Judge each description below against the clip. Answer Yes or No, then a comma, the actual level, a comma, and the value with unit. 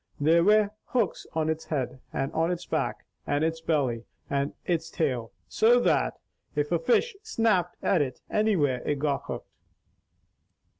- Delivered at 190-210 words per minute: No, average, 155 wpm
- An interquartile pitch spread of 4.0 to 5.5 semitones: Yes, average, 5.1 semitones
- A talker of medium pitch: Yes, medium, 160 Hz